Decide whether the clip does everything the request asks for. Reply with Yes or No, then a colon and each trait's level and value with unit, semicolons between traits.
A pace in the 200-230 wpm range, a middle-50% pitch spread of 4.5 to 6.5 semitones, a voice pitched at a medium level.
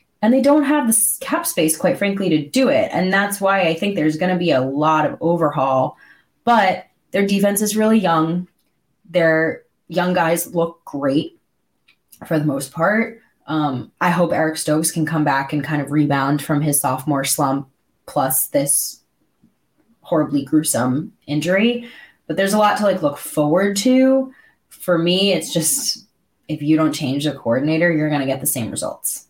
No: average, 180 wpm; average, 5.1 semitones; medium, 165 Hz